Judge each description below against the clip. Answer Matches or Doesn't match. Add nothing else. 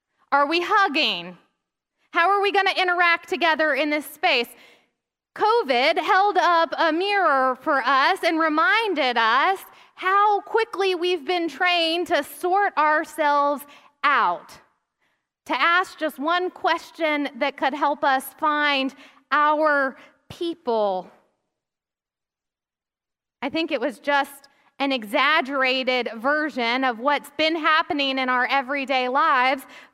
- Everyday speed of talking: Doesn't match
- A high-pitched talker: Matches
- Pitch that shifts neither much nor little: Matches